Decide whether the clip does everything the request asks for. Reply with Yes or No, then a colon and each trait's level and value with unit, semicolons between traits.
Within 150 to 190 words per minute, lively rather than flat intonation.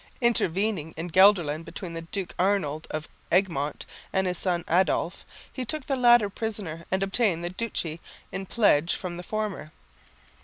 No: average, 155 wpm; average, 3.9 semitones